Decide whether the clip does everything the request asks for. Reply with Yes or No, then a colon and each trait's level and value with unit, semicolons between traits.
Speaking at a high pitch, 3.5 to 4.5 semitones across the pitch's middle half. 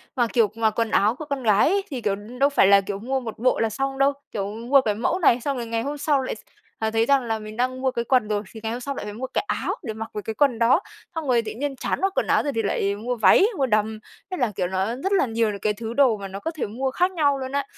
Yes: high, 235 Hz; average, 4.0 semitones